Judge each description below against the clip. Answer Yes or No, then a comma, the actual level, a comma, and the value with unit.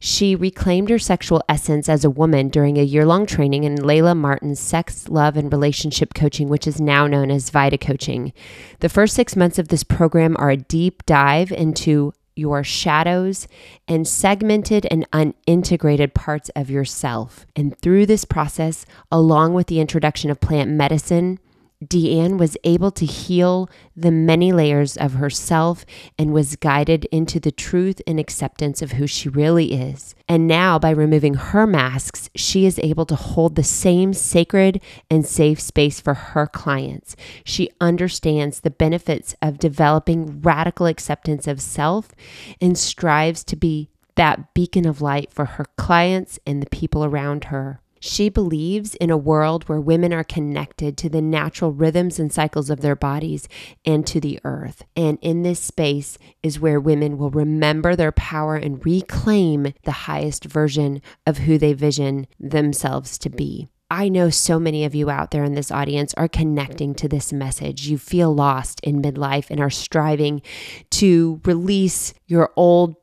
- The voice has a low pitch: No, medium, 155 Hz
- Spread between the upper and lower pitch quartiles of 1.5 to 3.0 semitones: Yes, narrow, 2.6 semitones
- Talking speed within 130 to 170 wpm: Yes, average, 165 wpm